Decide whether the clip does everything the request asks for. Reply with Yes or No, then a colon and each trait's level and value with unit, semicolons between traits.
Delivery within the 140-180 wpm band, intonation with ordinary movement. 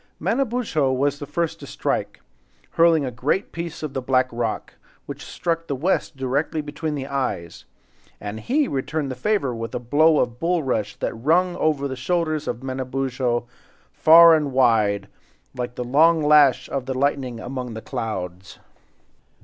Yes: average, 155 wpm; average, 4.4 semitones